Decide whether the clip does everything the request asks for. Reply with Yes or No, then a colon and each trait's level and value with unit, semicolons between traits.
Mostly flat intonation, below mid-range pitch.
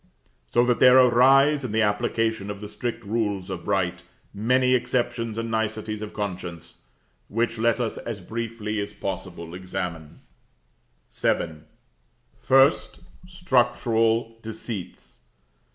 No: average, 3.5 semitones; low, 110 Hz